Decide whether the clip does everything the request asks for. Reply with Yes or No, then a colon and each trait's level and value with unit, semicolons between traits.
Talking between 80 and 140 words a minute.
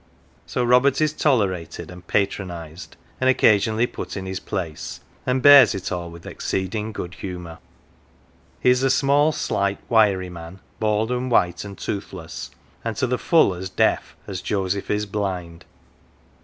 No: average, 155 wpm